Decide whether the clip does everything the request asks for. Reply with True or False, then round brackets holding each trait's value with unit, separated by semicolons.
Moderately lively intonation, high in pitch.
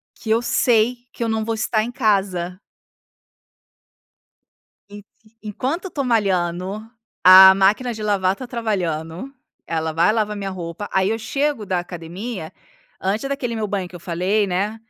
True (3.7 semitones; 205 Hz)